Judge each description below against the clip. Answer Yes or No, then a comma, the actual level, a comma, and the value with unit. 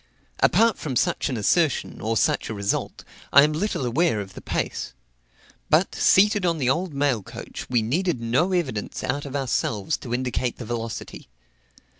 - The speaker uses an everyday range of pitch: No, wide, 6.3 semitones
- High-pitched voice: No, low, 130 Hz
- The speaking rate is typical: Yes, average, 170 wpm